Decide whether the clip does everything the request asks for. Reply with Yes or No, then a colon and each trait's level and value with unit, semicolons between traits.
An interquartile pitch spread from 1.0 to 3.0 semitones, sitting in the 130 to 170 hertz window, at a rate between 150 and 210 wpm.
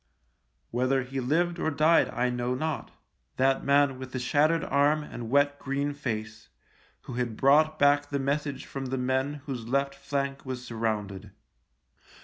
Yes: narrow, 2.5 semitones; low, 135 Hz; average, 165 wpm